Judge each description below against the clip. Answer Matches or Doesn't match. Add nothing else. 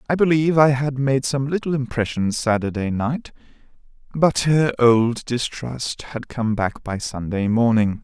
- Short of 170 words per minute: Matches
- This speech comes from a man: Matches